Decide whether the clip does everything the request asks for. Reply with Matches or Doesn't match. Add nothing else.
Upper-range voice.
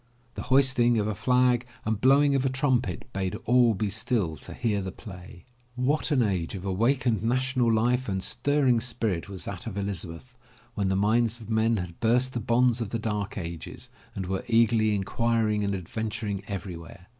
Doesn't match